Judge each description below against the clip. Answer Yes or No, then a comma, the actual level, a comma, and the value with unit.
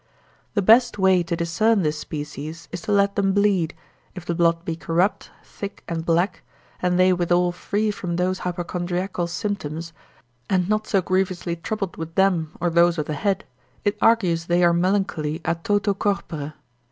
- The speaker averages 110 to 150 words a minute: No, average, 170 wpm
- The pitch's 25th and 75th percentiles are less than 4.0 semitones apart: Yes, average, 2.9 semitones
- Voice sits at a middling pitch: Yes, medium, 180 Hz